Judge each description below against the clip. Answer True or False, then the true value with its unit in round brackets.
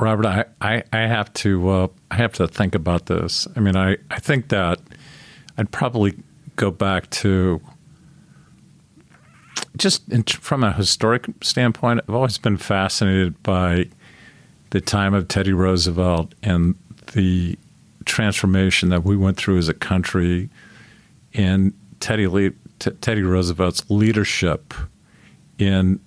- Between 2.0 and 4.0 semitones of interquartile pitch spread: True (3.1 semitones)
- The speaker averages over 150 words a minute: False (135 wpm)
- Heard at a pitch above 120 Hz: False (100 Hz)